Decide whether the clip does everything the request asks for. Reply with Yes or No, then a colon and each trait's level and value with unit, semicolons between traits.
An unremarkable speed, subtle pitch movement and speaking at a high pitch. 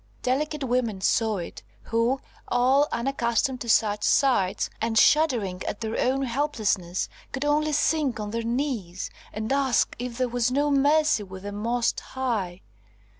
No: average, 150 wpm; average, 4.2 semitones; high, 240 Hz